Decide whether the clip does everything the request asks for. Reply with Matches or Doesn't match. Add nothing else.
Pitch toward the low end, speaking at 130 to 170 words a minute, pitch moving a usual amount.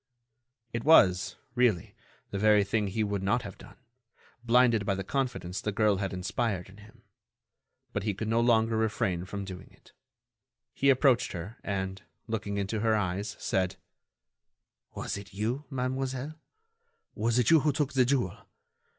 Matches